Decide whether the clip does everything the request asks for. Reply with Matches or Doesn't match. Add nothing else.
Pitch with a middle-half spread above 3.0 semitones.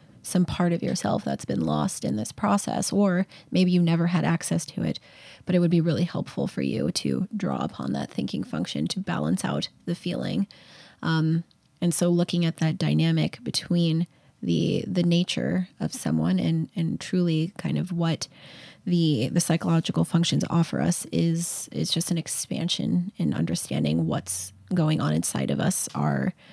Doesn't match